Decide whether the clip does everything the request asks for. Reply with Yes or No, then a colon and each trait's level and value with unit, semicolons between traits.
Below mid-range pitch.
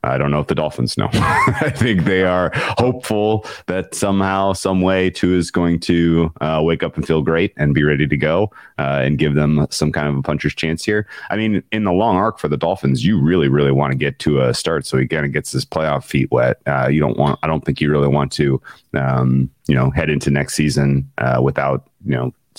Yes: very low, 75 Hz